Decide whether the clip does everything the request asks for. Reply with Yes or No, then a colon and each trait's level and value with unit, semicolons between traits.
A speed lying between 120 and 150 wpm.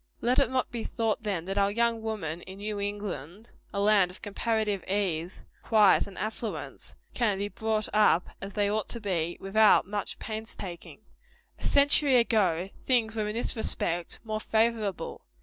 No: average, 170 wpm